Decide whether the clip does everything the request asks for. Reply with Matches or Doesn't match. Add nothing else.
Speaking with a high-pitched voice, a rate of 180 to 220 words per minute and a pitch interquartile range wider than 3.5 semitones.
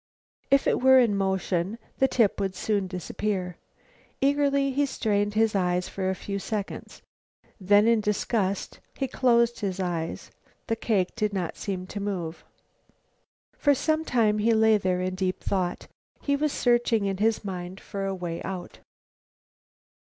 Doesn't match